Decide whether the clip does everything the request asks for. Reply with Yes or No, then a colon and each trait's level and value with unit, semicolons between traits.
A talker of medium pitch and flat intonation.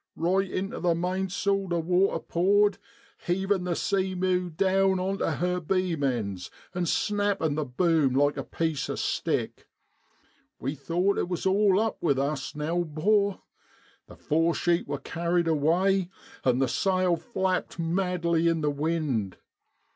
No: medium, 175 Hz; average, 3.4 semitones